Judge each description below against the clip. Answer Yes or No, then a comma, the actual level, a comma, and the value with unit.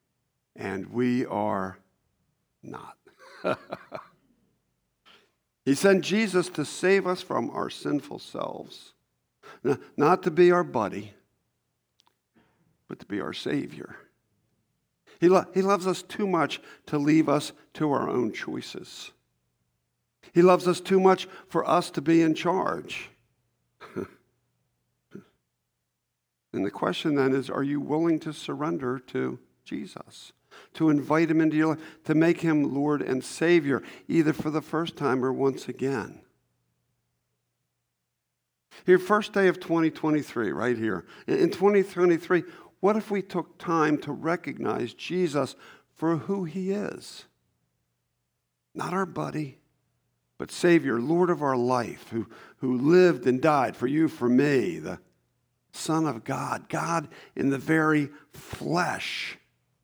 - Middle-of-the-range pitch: Yes, medium, 155 Hz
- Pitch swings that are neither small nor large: No, wide, 6.5 semitones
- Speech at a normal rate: No, slow, 130 wpm